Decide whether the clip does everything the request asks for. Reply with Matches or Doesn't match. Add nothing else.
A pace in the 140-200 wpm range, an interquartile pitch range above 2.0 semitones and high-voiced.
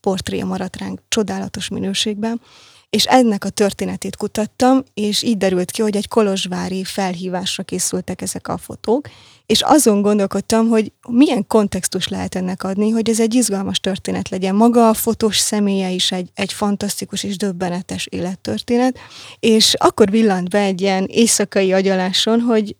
Matches